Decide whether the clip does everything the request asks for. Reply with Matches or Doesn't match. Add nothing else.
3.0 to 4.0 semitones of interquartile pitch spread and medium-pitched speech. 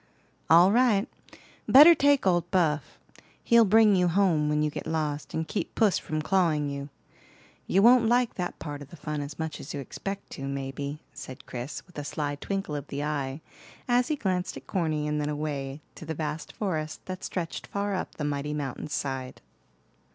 Doesn't match